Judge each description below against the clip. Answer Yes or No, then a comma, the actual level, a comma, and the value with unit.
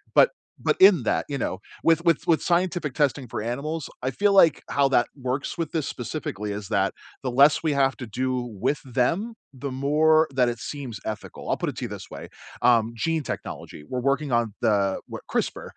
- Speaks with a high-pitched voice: No, low, 135 Hz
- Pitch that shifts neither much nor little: Yes, average, 4.5 semitones